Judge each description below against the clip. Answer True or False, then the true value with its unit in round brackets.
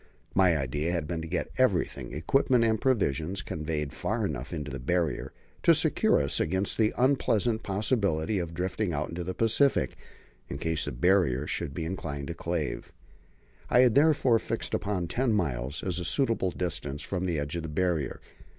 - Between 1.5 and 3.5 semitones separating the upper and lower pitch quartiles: False (5.5 semitones)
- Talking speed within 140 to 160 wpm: False (180 wpm)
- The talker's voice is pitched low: True (85 Hz)